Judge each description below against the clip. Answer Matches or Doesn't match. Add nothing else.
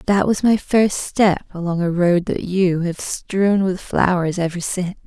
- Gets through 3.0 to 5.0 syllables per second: Matches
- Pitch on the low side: Doesn't match